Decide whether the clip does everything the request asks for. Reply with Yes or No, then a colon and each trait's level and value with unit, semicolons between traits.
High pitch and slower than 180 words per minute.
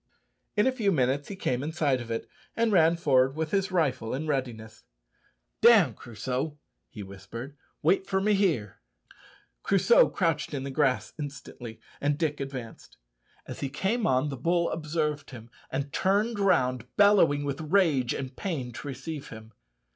No: medium, 145 Hz; average, 160 wpm